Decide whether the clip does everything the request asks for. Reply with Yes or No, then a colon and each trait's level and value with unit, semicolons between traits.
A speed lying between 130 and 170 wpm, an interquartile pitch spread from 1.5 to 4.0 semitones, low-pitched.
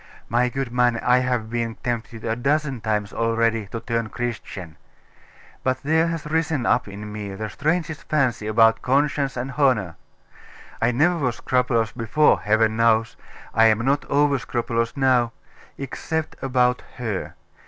Yes: average, 150 wpm; average, 3.3 semitones; low, 120 Hz